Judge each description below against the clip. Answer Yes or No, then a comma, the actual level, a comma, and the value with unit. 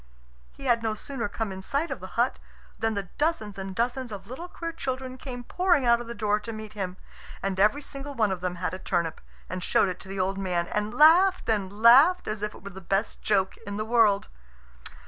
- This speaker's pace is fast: Yes, fast, 230 wpm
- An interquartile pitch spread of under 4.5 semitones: No, average, 4.9 semitones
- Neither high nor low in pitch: No, high, 215 Hz